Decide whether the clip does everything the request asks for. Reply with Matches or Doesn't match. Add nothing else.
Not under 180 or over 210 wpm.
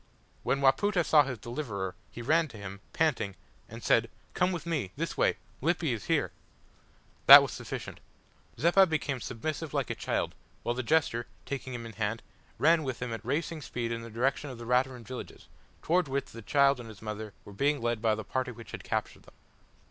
Matches